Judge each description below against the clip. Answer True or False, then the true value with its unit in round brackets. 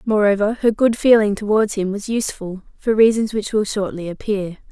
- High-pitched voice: True (210 Hz)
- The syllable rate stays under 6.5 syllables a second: True (5.3 syllables/s)